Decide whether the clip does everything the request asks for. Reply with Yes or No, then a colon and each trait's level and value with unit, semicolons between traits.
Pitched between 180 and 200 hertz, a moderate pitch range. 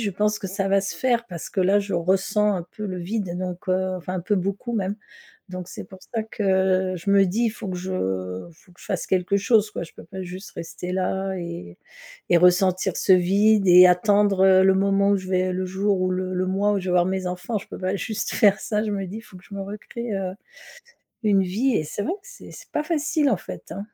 No: high, 190 Hz; narrow, 2.0 semitones